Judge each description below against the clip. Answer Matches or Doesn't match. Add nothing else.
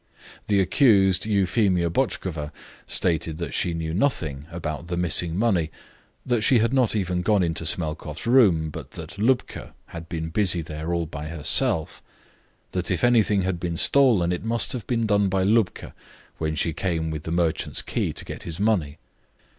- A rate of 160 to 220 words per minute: Matches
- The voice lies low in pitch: Matches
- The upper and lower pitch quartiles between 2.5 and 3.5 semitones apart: Doesn't match